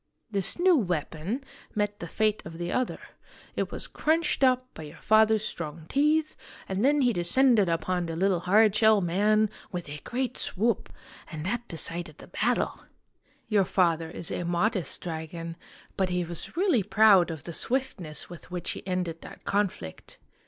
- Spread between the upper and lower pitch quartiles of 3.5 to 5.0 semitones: Yes, average, 4.7 semitones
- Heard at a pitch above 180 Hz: Yes, high, 190 Hz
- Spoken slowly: No, average, 165 wpm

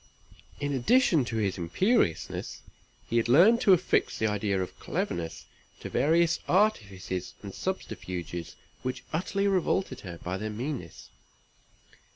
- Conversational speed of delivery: No, slow, 130 wpm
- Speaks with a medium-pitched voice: No, low, 120 Hz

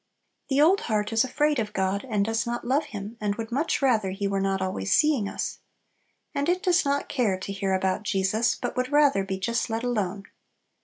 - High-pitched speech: Yes, high, 225 Hz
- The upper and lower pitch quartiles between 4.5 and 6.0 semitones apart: Yes, wide, 5.4 semitones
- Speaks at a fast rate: Yes, fast, 210 wpm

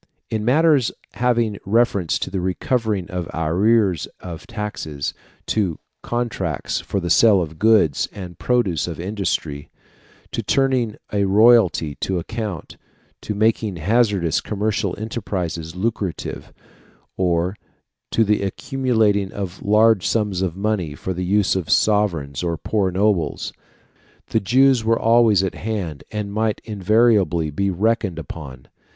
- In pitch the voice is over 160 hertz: No, low, 100 Hz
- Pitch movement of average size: Yes, average, 4.1 semitones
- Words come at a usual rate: No, slow, 130 wpm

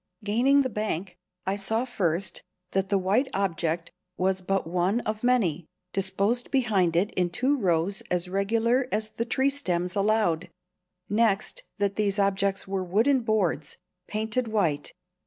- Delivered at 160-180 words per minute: No, average, 145 wpm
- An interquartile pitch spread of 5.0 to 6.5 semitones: No, average, 3.6 semitones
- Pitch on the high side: Yes, high, 200 Hz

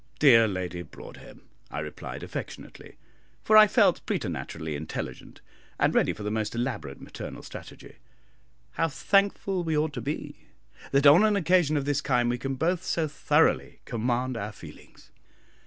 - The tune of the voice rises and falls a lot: Yes, wide, 6.2 semitones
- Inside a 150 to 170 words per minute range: Yes, average, 155 wpm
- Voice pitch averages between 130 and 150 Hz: Yes, low, 135 Hz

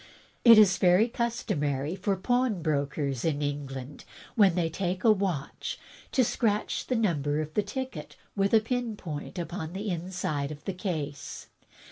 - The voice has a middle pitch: Yes, medium, 180 Hz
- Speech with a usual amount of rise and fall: No, wide, 6.1 semitones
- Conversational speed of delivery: Yes, average, 150 wpm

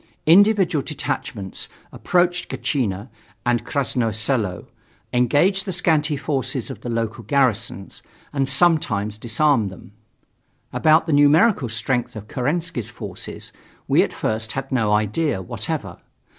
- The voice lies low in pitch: Yes, low, 130 Hz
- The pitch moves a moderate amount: No, wide, 5.8 semitones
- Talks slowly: Yes, slow, 120 wpm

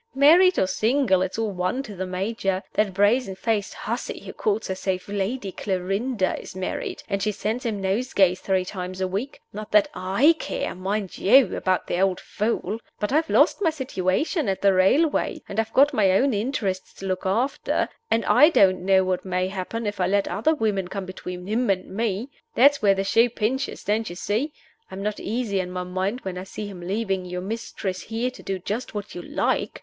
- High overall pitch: Yes, high, 200 Hz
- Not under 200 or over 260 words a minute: Yes, fast, 205 wpm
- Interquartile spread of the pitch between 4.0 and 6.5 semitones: No, average, 3.5 semitones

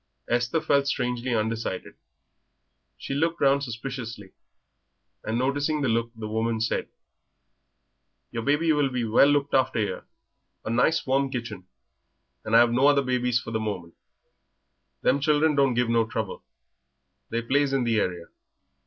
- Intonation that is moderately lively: Yes, average, 3.7 semitones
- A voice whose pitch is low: Yes, low, 125 Hz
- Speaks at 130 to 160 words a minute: Yes, average, 145 wpm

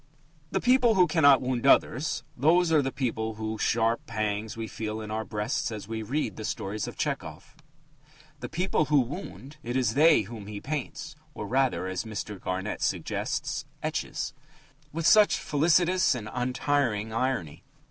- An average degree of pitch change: No, wide, 5.9 semitones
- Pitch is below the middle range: Yes, low, 125 Hz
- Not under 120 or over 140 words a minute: No, average, 160 wpm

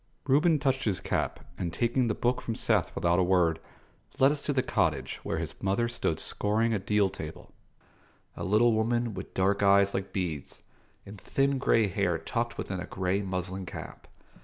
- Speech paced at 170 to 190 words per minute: Yes, average, 185 wpm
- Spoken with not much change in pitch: No, average, 4.1 semitones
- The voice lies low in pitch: Yes, low, 100 Hz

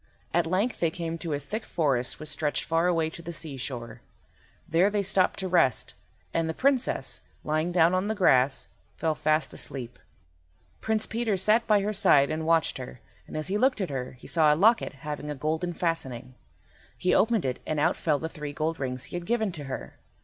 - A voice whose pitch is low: No, medium, 165 Hz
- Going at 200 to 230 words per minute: Yes, fast, 205 wpm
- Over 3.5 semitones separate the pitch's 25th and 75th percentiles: Yes, average, 4.3 semitones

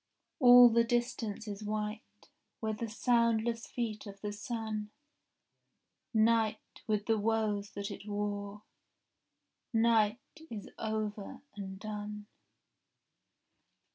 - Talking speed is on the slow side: Yes, slow, 105 wpm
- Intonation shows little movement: Yes, narrow, 1.7 semitones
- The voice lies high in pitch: Yes, high, 215 Hz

